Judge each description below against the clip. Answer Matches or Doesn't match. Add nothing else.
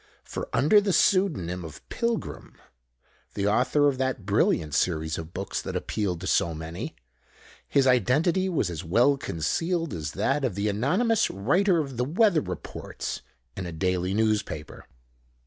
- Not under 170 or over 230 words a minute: Doesn't match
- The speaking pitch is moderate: Doesn't match